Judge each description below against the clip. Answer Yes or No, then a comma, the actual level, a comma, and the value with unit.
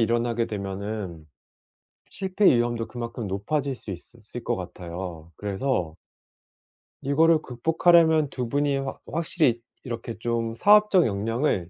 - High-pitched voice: No, low, 120 Hz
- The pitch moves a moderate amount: No, wide, 6.2 semitones